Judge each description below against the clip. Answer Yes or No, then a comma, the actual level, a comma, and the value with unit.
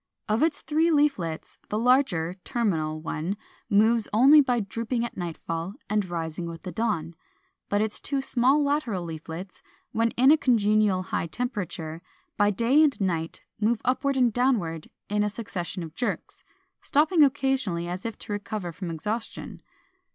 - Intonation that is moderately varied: No, wide, 6.3 semitones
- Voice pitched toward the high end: Yes, high, 210 Hz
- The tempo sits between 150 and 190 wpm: Yes, average, 160 wpm